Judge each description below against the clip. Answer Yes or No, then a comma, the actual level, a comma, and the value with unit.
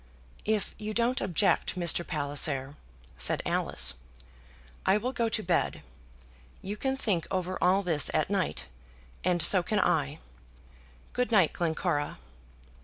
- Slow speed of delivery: Yes, slow, 130 wpm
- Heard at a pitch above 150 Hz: Yes, medium, 185 Hz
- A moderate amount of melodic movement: Yes, average, 4.4 semitones